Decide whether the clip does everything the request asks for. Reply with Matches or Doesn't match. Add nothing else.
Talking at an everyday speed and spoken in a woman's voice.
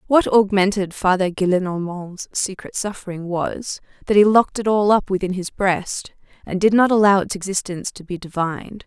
Matches